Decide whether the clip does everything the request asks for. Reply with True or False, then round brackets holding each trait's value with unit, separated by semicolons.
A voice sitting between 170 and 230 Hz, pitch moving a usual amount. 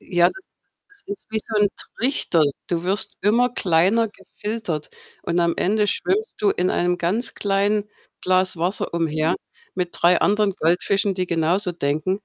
True (190 Hz; 3.4 semitones)